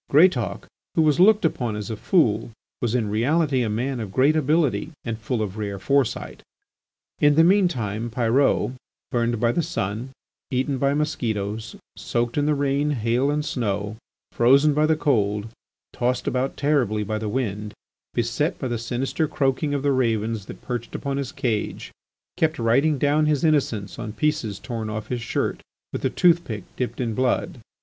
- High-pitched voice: No, low, 125 Hz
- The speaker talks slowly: No, average, 175 wpm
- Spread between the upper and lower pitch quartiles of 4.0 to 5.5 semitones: Yes, average, 4.9 semitones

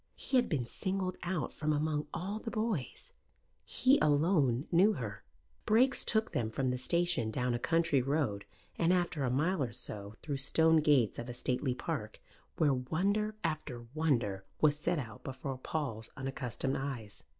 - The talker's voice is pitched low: No, medium, 145 Hz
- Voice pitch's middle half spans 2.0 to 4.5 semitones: No, wide, 5.6 semitones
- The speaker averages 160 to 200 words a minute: Yes, average, 165 wpm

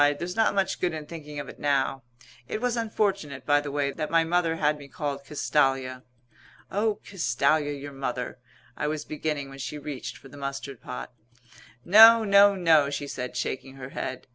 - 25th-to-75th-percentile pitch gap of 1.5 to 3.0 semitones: No, average, 3.7 semitones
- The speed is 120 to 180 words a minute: No, average, 190 wpm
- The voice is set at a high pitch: No, medium, 145 Hz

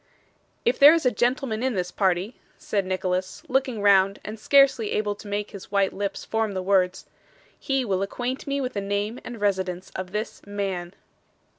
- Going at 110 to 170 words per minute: No, average, 180 wpm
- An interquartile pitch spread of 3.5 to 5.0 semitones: Yes, average, 4.2 semitones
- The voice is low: No, high, 205 Hz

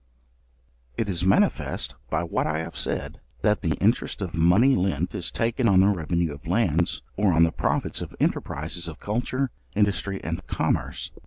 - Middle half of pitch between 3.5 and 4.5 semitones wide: Yes, average, 4.1 semitones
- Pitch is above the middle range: No, very low, 95 Hz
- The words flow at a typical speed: Yes, average, 170 wpm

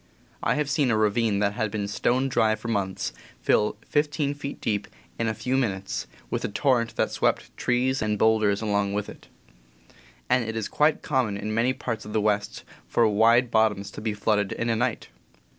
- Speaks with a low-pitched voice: Yes, low, 110 Hz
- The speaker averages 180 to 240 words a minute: Yes, average, 200 wpm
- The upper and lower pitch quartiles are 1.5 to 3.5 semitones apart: Yes, average, 3.2 semitones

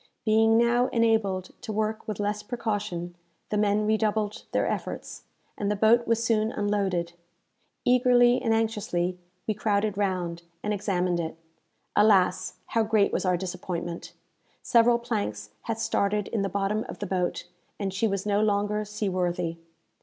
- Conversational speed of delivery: Yes, average, 155 wpm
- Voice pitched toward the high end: Yes, high, 210 Hz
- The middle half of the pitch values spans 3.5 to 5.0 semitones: No, average, 2.9 semitones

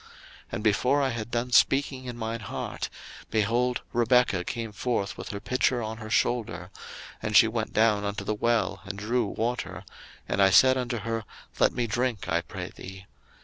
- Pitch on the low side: Yes, low, 115 Hz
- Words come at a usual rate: Yes, average, 185 wpm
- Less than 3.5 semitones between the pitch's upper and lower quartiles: Yes, average, 3.0 semitones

